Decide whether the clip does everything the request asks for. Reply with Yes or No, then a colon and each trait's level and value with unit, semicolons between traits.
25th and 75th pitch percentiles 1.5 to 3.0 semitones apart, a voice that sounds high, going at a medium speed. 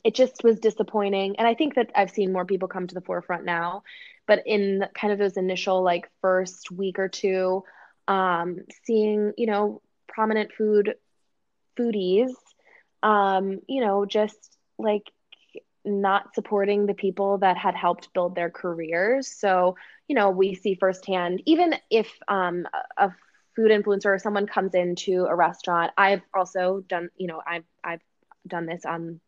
Yes: narrow, 2.6 semitones; high, 195 Hz; average, 160 wpm